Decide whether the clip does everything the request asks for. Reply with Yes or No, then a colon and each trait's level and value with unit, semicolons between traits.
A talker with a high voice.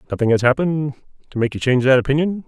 No: low, 135 Hz